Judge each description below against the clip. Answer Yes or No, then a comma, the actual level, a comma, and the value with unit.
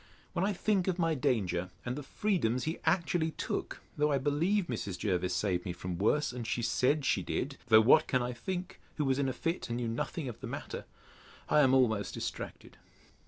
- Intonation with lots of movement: Yes, wide, 6.1 semitones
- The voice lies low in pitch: Yes, low, 130 Hz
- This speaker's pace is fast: Yes, fast, 210 wpm